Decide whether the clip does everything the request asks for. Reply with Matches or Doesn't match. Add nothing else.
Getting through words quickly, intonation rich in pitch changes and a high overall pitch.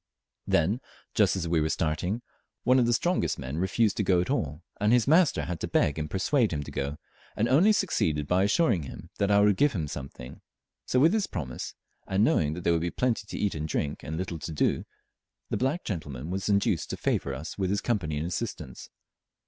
Doesn't match